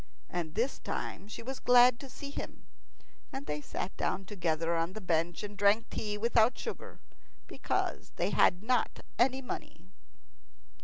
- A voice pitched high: Yes, high, 210 Hz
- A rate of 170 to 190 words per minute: No, average, 155 wpm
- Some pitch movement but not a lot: No, wide, 5.7 semitones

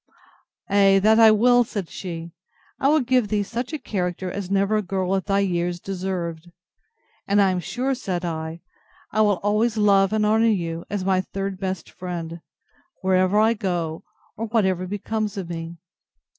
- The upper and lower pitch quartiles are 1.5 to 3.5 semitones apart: Yes, average, 3.1 semitones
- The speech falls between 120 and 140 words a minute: No, average, 170 wpm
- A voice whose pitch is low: No, high, 195 Hz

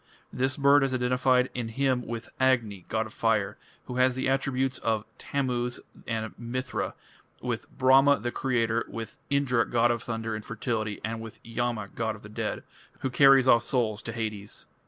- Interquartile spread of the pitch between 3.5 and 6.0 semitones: No, narrow, 2.5 semitones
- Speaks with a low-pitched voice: Yes, low, 120 Hz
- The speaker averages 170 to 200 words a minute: Yes, average, 175 wpm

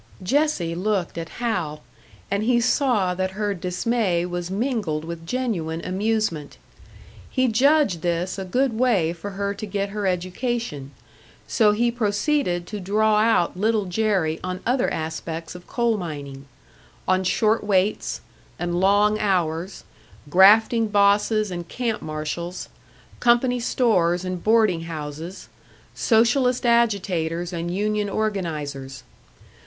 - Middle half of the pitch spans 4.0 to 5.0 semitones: Yes, average, 4.5 semitones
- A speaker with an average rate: No, slow, 125 wpm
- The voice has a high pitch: Yes, high, 195 Hz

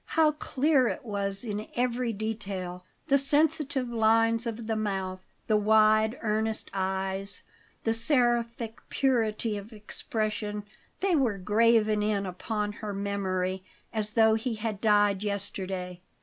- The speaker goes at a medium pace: No, slow, 130 wpm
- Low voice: No, high, 215 Hz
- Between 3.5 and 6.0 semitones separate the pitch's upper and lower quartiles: No, narrow, 2.5 semitones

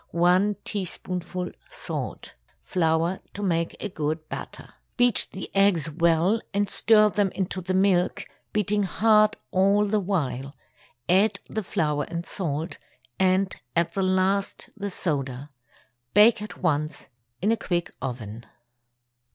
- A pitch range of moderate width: Yes, average, 3.7 semitones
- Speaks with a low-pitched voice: No, medium, 185 Hz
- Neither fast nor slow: No, slow, 125 wpm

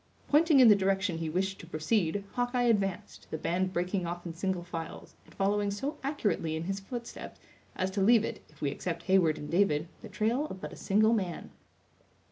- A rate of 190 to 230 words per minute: Yes, average, 200 wpm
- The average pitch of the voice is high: Yes, high, 195 Hz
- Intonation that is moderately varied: Yes, average, 4.1 semitones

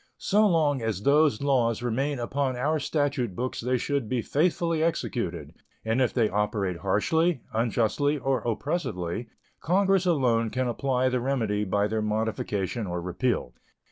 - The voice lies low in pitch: Yes, low, 125 Hz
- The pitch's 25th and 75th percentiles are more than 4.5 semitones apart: Yes, average, 5.1 semitones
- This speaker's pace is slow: No, average, 145 wpm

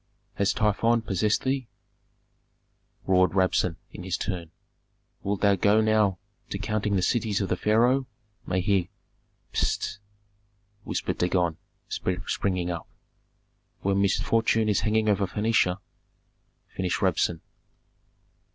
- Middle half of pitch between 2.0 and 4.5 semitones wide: Yes, average, 2.8 semitones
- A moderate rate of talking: No, slow, 120 wpm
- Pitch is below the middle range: Yes, low, 100 Hz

